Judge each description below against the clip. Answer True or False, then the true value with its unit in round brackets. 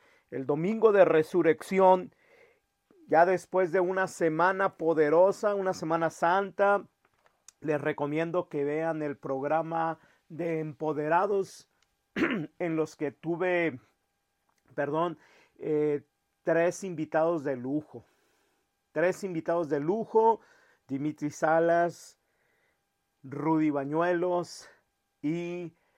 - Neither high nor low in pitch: True (165 Hz)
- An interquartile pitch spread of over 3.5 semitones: False (3.2 semitones)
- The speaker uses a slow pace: True (90 wpm)